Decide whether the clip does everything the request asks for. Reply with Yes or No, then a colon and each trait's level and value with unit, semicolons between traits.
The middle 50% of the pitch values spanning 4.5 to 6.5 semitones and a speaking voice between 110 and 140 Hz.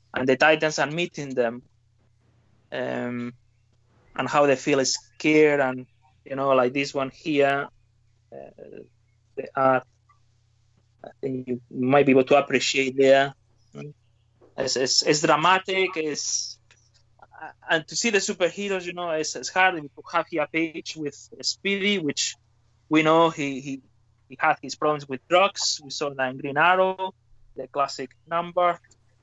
Yes: average, 5.1 semitones; low, 135 Hz